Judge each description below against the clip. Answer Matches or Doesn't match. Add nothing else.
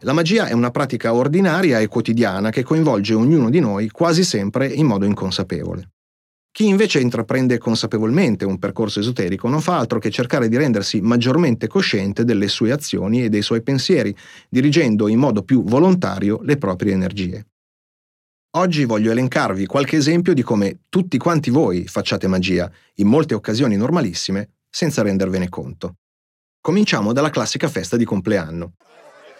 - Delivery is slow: Doesn't match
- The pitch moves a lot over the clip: Matches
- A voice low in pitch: Matches